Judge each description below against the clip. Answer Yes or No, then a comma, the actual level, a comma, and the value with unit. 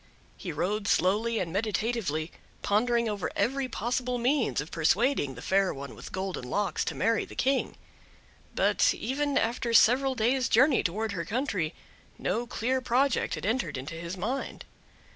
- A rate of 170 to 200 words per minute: No, average, 155 wpm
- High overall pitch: Yes, high, 225 Hz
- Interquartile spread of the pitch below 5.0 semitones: No, average, 5.3 semitones